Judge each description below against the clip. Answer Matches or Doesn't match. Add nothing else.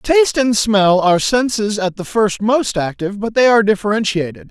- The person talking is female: Doesn't match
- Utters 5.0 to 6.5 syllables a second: Matches